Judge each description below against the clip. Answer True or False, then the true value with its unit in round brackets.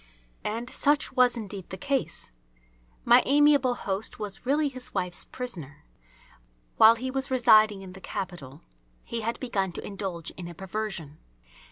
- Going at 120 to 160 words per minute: True (150 wpm)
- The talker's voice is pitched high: True (215 Hz)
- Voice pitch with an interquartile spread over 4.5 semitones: True (5.1 semitones)